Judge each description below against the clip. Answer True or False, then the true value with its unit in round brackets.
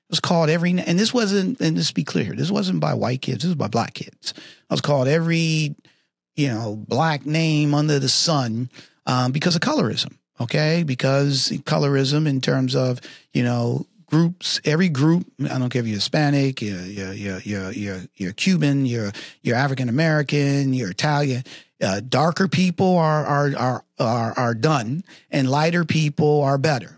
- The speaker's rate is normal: True (175 wpm)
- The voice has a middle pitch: True (145 Hz)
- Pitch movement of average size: True (4.2 semitones)